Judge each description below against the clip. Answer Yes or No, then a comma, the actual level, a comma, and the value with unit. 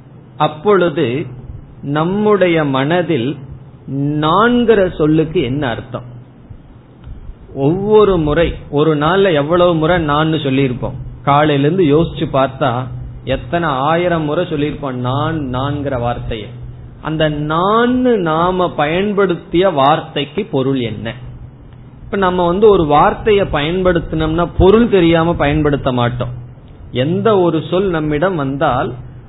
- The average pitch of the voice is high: No, medium, 150 Hz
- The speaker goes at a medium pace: Yes, average, 90 wpm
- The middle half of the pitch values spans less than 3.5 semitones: No, average, 4.8 semitones